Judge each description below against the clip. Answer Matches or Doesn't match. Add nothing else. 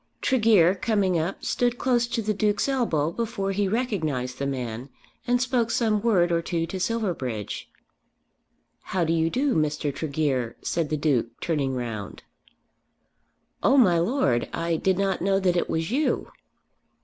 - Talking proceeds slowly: Doesn't match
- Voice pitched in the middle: Matches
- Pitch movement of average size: Doesn't match